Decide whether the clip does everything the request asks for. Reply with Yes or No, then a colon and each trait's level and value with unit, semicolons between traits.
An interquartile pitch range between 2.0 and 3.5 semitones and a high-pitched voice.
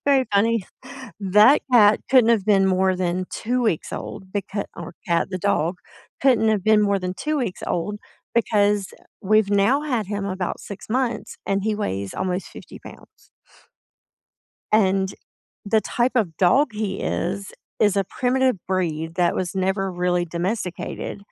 Yes: average, 2.9 semitones; high, 200 Hz